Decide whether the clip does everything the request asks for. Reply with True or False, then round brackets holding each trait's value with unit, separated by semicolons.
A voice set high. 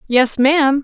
True (270 Hz)